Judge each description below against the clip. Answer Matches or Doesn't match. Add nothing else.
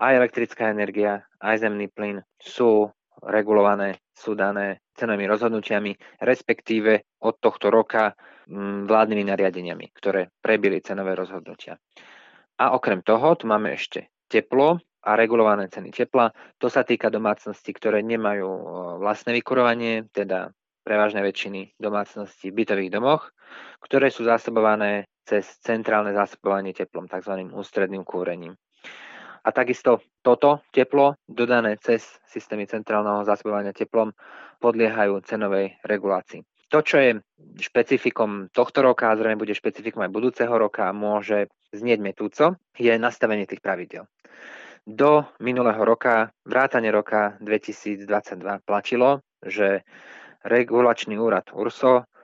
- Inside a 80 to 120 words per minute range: Matches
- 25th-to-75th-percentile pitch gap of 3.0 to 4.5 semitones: Doesn't match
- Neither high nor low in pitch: Doesn't match